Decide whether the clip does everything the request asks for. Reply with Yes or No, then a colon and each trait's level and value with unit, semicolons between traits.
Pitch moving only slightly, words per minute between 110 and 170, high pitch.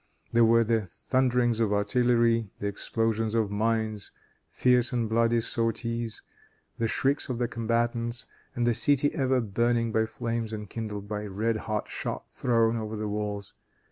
No: narrow, 1.6 semitones; average, 150 wpm; low, 115 Hz